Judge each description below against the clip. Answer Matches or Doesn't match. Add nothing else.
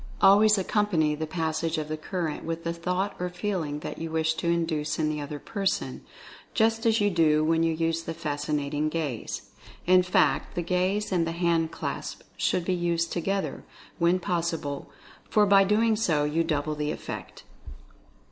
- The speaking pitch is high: Doesn't match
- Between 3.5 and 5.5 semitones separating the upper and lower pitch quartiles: Doesn't match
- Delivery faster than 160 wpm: Matches